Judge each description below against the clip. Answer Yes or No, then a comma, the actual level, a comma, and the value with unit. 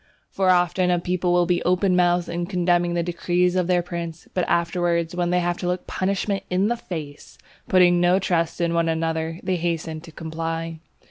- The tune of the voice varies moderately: No, narrow, 1.2 semitones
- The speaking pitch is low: No, medium, 175 Hz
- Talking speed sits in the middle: Yes, average, 195 wpm